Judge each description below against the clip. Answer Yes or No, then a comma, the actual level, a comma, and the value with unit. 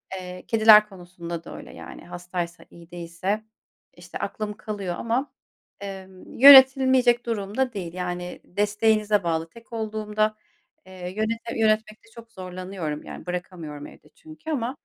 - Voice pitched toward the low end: No, high, 205 Hz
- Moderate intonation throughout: Yes, average, 4.1 semitones